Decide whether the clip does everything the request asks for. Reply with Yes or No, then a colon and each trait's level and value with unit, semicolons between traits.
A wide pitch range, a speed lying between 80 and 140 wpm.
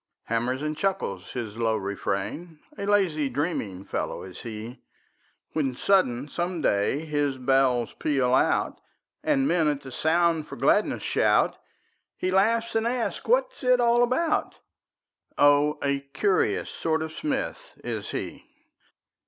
Yes: wide, 7.6 semitones; slow, 135 wpm